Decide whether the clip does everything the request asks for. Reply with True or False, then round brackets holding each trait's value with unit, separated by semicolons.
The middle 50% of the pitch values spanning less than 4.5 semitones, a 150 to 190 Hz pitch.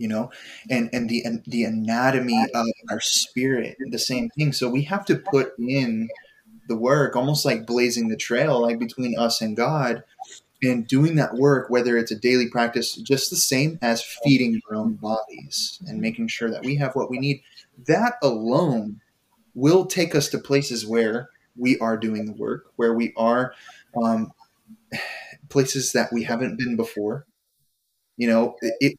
False (3.4 semitones; 125 Hz)